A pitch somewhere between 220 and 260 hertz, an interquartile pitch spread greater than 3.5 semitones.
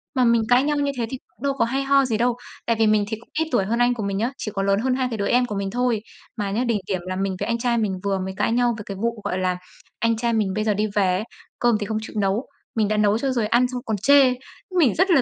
No: high, 230 Hz; average, 3.2 semitones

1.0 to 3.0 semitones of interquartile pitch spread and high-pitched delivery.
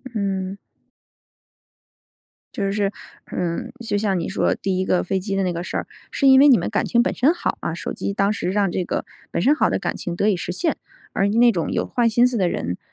No: average, 3.8 semitones; high, 200 Hz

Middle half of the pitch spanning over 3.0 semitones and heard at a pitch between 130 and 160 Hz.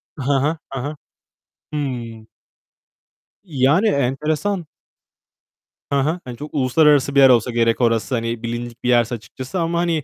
Yes: average, 4.2 semitones; low, 135 Hz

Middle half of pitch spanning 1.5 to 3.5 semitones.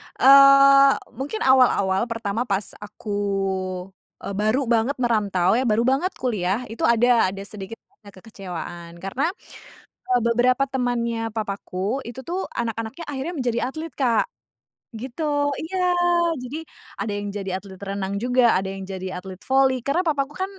No: average, 5.1 semitones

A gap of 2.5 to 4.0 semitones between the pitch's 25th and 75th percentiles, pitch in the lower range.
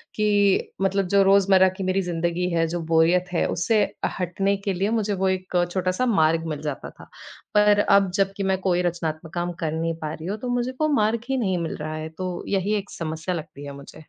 No: average, 3.2 semitones; medium, 185 Hz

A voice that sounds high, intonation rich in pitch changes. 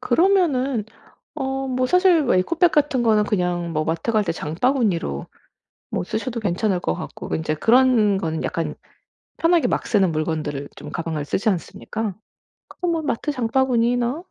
Yes: high, 225 Hz; wide, 7.3 semitones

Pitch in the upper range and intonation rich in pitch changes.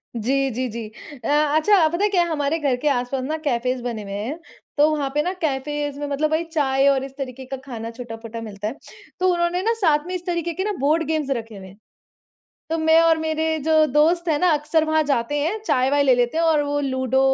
No: very high, 290 Hz; average, 3.9 semitones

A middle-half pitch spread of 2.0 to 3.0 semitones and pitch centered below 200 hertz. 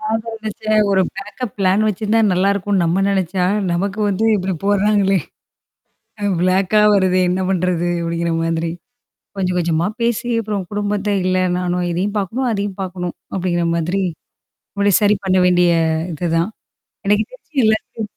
Yes: narrow, 2.6 semitones; high, 190 Hz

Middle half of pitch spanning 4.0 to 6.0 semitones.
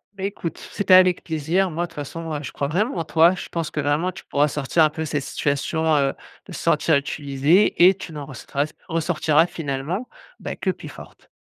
No: average, 3.4 semitones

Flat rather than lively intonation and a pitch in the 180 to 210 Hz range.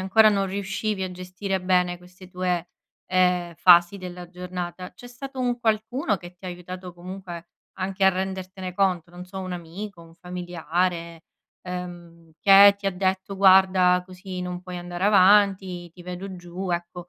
Yes: narrow, 1.4 semitones; medium, 185 Hz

